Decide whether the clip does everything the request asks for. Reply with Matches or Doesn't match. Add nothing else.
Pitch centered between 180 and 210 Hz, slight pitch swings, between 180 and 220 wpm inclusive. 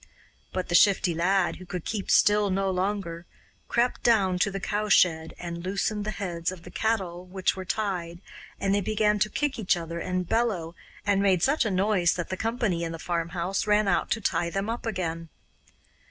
Doesn't match